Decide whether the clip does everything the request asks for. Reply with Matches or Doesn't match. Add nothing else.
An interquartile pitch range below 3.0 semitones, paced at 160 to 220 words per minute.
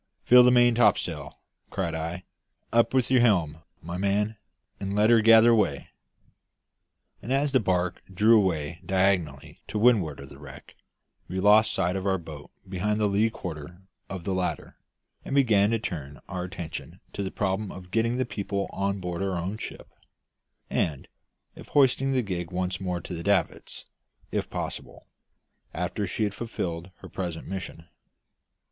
Doesn't match